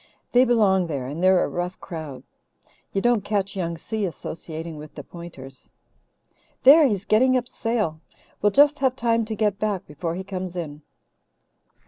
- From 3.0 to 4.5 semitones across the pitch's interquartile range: No, wide, 5.4 semitones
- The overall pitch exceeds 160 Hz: Yes, high, 190 Hz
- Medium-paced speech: Yes, average, 165 wpm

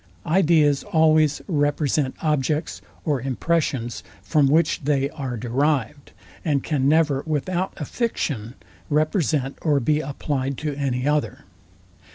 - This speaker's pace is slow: Yes, slow, 125 wpm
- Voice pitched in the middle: Yes, medium, 145 Hz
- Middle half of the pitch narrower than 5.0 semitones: Yes, narrow, 2.5 semitones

